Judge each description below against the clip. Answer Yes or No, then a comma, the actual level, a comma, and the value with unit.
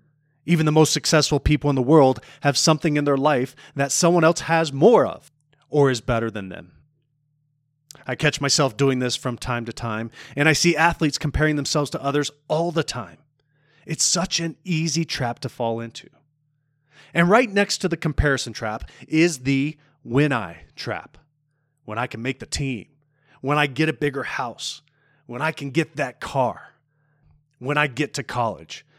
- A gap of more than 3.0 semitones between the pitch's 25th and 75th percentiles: No, narrow, 2.4 semitones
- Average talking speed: Yes, average, 180 wpm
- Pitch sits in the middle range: Yes, medium, 145 Hz